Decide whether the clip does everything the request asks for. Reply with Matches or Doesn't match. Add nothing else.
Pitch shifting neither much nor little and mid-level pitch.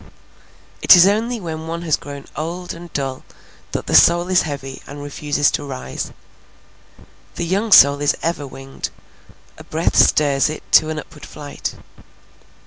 Matches